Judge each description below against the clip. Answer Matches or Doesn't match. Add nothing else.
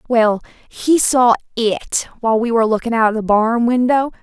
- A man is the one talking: Doesn't match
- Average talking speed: Matches